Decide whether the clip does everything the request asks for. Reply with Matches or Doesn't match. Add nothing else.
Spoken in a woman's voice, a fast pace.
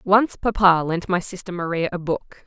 Doesn't match